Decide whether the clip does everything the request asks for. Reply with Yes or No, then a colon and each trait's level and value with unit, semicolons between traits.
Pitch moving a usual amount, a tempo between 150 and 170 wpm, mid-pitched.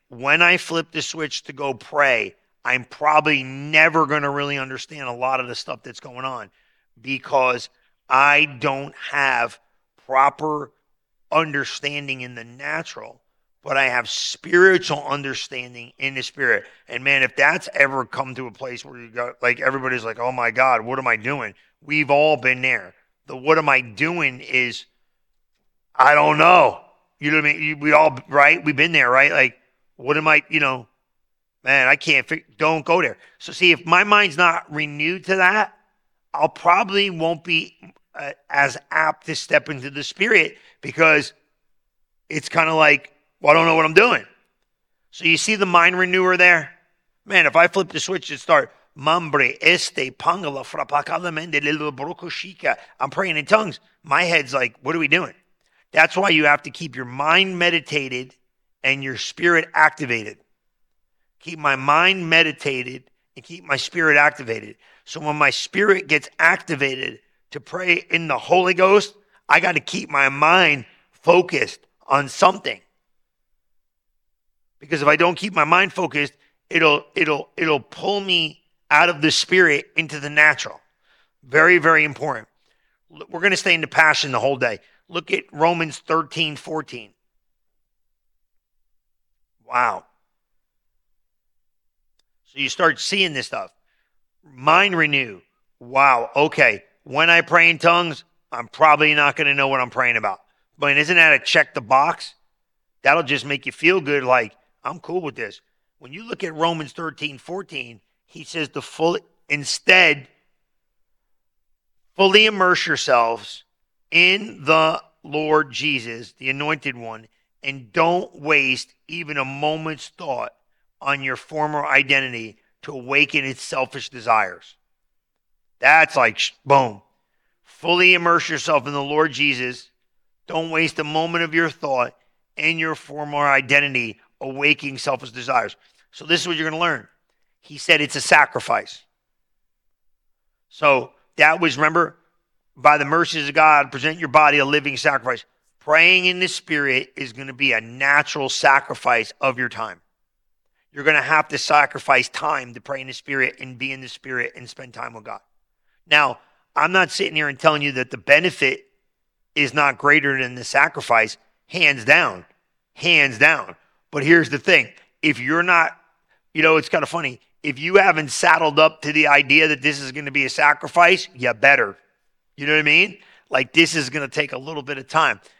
Yes: average, 3.4 semitones; average, 165 wpm; medium, 150 Hz